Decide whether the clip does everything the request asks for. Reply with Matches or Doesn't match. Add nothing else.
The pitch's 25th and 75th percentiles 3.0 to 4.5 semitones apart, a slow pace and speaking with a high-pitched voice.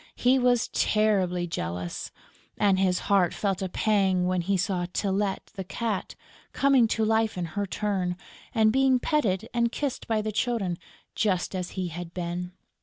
Doesn't match